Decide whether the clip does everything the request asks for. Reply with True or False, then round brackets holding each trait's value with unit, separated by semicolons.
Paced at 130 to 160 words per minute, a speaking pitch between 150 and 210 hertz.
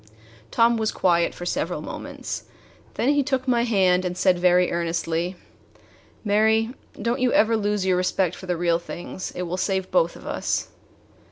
False (170 wpm; 190 Hz)